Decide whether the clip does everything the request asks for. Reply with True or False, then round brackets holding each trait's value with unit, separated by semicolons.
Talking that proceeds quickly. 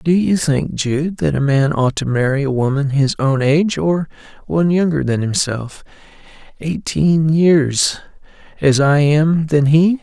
False (150 wpm)